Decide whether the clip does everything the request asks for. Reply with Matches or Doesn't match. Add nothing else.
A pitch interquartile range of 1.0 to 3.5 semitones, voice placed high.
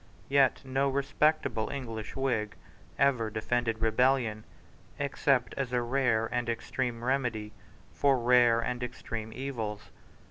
Doesn't match